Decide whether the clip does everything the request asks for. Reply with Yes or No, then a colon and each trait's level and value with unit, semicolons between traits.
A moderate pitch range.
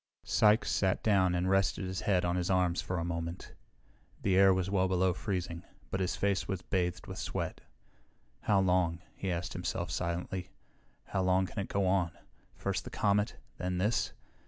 No: narrow, 1.6 semitones